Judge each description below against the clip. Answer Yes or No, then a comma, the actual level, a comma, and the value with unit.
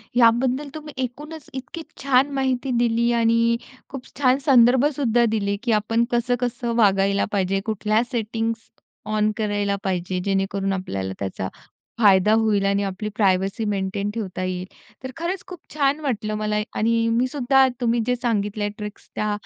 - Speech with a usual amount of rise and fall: Yes, average, 3.8 semitones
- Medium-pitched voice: No, high, 225 Hz